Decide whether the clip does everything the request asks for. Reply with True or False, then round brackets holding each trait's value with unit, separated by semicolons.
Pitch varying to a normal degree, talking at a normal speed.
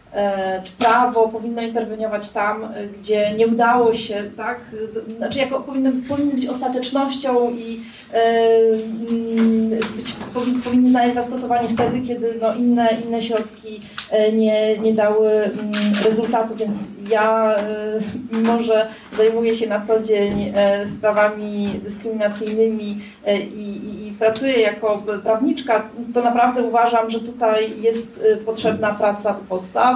False (1.7 semitones; 125 wpm)